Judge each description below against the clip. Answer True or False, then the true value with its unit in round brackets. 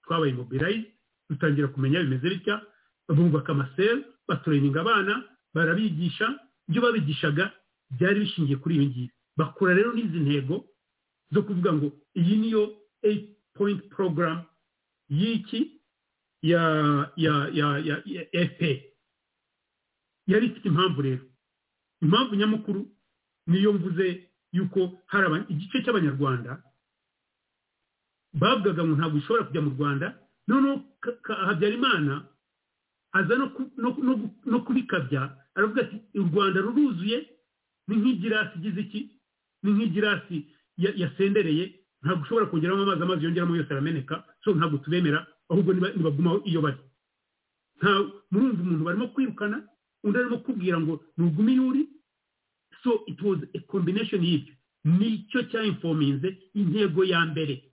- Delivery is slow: True (110 wpm)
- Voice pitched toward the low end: False (185 Hz)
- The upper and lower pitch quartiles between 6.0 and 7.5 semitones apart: False (5.2 semitones)